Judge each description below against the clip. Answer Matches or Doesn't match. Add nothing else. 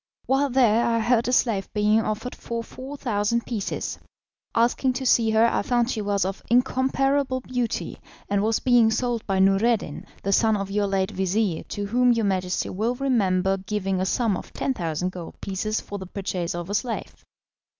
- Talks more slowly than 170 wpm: Doesn't match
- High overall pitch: Matches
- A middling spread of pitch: Matches